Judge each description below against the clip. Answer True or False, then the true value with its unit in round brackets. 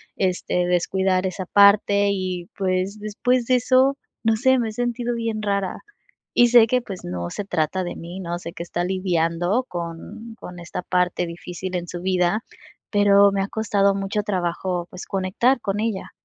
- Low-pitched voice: False (195 Hz)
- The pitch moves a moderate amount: True (3.3 semitones)